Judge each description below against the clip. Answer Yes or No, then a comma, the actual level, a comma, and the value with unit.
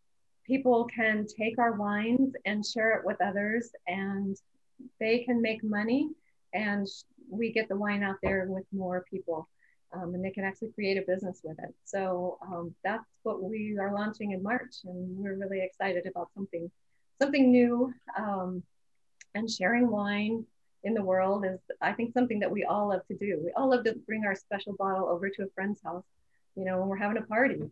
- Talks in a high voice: Yes, high, 205 Hz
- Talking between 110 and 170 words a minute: No, average, 195 wpm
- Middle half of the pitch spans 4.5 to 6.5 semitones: No, average, 3.0 semitones